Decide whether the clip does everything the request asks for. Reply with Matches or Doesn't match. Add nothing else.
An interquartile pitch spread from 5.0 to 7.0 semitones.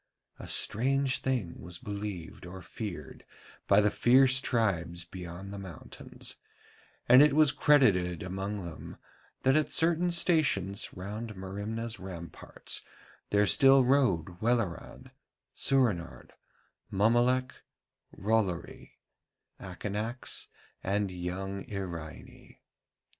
Matches